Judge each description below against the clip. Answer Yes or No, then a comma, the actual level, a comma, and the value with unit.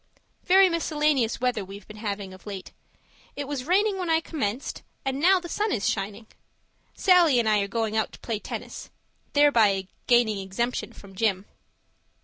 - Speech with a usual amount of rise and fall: No, wide, 7.2 semitones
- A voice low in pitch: No, high, 235 Hz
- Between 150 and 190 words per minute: Yes, average, 160 wpm